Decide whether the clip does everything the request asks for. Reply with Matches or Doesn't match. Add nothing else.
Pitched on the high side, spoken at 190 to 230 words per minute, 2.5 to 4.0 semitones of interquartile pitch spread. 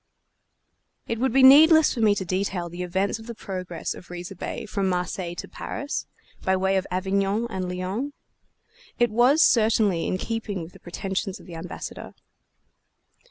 Doesn't match